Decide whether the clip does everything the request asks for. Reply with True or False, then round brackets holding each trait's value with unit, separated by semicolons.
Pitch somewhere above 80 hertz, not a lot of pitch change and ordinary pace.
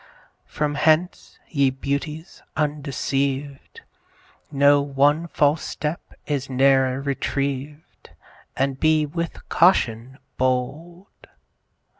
False (140 Hz; 2.3 semitones; 85 wpm)